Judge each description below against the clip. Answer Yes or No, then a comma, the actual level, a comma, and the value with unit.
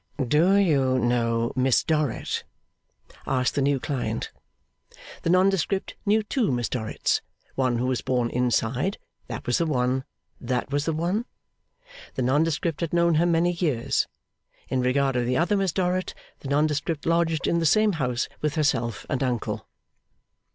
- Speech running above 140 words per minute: Yes, average, 155 wpm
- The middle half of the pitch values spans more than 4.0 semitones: Yes, average, 5.1 semitones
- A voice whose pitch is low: No, medium, 145 Hz